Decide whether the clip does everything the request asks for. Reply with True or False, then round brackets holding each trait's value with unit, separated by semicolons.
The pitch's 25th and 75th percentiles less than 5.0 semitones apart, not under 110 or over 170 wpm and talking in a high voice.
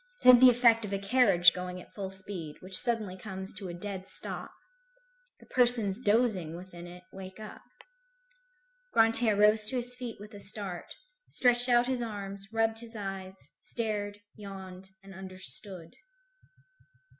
True (3.3 semitones; 155 wpm; 205 Hz)